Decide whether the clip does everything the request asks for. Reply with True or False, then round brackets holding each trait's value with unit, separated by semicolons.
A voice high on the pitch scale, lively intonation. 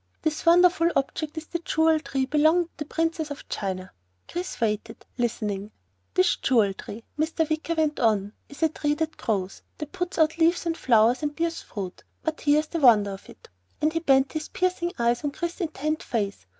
True (300 Hz; 6.0 semitones)